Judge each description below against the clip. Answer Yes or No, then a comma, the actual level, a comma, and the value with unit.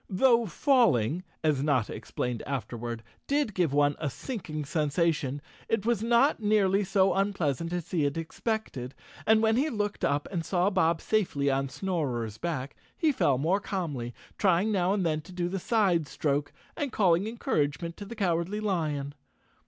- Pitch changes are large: Yes, wide, 6.2 semitones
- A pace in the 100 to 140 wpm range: No, average, 165 wpm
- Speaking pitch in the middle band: Yes, medium, 175 Hz